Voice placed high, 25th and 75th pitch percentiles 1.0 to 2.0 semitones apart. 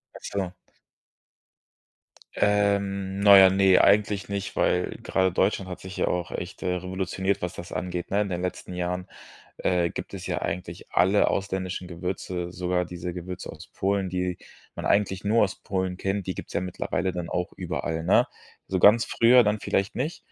No: very low, 95 Hz; narrow, 1.7 semitones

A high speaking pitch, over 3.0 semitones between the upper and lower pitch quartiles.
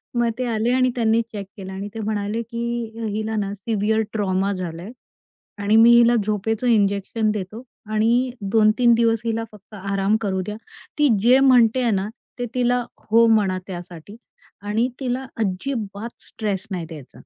No: high, 220 Hz; average, 2.7 semitones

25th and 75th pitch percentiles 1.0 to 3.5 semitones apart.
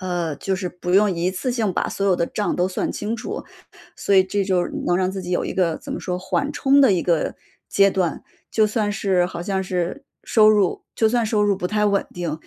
Yes: average, 2.8 semitones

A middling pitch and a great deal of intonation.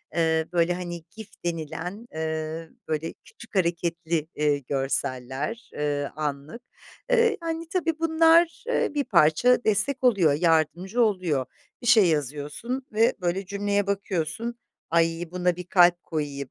Yes: medium, 175 Hz; wide, 6.5 semitones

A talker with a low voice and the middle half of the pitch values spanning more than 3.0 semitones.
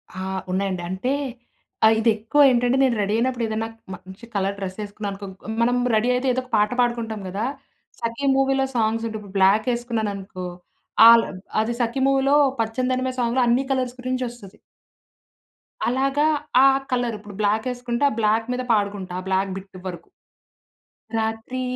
No: high, 230 Hz; average, 3.6 semitones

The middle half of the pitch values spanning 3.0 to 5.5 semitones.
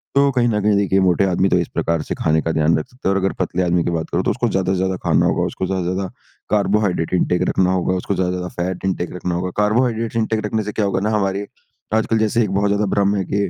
No: narrow, 2.6 semitones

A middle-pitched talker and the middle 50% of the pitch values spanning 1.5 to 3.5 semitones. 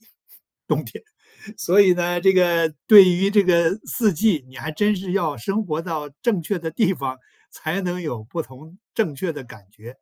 No: medium, 175 Hz; average, 4.1 semitones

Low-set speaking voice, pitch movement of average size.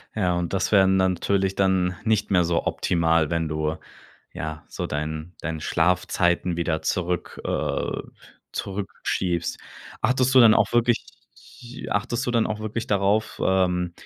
Yes: very low, 90 Hz; average, 3.6 semitones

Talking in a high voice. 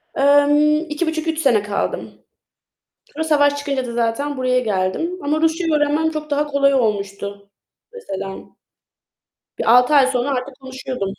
Yes: very high, 280 Hz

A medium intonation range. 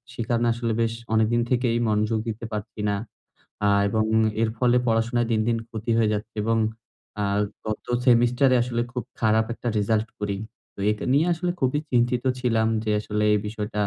No: narrow, 1.8 semitones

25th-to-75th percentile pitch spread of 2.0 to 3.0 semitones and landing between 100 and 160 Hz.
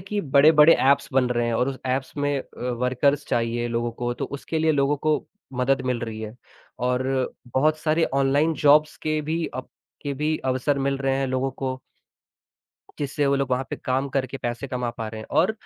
Yes: average, 2.7 semitones; low, 135 Hz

